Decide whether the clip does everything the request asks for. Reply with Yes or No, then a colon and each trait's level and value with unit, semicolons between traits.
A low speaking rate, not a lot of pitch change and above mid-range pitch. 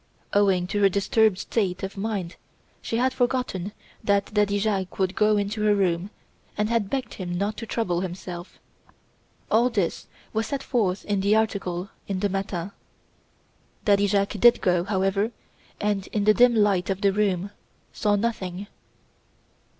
No: average, 160 wpm; narrow, 2.2 semitones; high, 200 Hz